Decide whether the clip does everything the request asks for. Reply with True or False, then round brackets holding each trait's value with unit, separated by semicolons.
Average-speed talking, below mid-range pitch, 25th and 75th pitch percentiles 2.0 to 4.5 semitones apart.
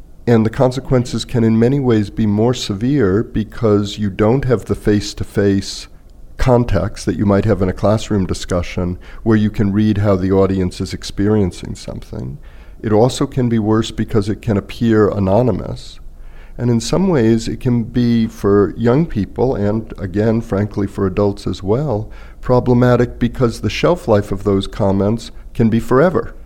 True (170 wpm; 105 Hz; 3.0 semitones)